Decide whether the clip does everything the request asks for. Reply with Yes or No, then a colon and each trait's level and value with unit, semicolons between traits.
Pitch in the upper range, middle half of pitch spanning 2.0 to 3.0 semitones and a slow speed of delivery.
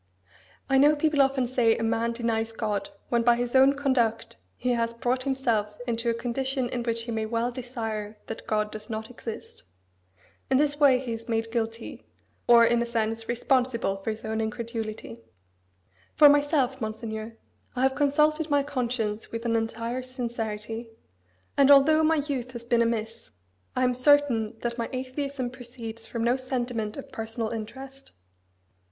No: high, 235 Hz; average, 2.7 semitones; average, 165 wpm